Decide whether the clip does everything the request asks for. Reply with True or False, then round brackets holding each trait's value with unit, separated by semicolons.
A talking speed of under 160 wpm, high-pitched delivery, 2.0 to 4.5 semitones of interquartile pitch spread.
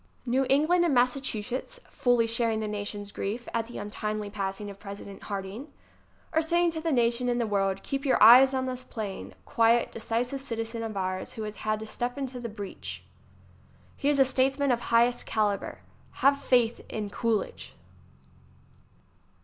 False (175 wpm; 235 Hz; 3.8 semitones)